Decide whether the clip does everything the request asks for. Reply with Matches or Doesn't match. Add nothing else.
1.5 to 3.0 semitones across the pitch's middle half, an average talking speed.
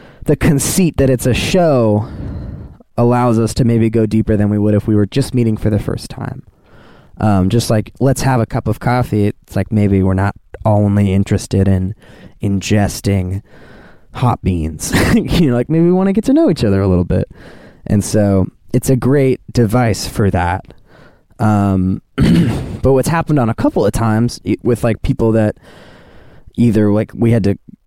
Doesn't match